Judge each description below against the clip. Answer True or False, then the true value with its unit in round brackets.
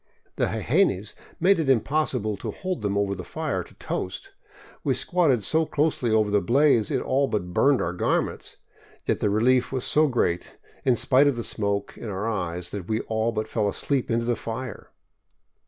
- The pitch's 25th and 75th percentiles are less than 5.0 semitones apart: False (5.3 semitones)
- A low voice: True (115 Hz)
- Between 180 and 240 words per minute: True (190 wpm)